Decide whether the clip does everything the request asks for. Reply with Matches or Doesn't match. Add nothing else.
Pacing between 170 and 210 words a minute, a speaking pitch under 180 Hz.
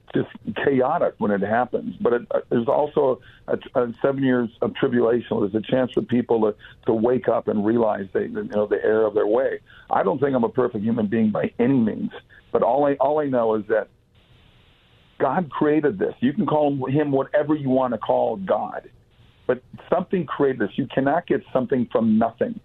Matches